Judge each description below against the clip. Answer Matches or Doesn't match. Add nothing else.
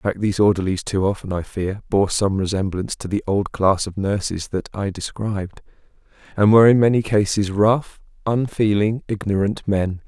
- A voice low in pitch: Matches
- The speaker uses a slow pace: Doesn't match